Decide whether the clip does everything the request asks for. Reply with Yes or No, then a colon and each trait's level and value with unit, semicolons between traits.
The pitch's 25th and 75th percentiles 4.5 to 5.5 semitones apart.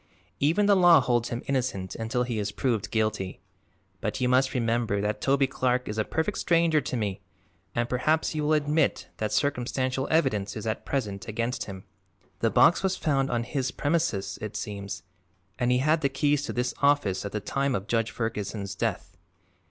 Yes: average, 5.0 semitones